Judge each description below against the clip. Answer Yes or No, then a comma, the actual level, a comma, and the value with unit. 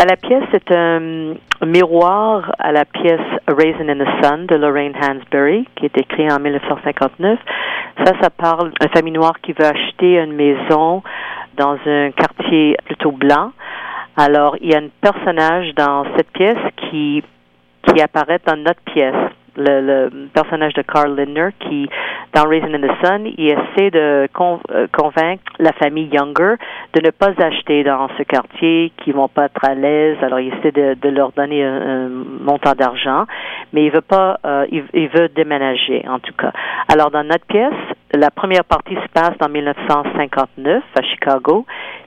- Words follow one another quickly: No, average, 170 wpm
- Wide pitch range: No, average, 2.7 semitones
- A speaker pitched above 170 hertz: No, medium, 150 Hz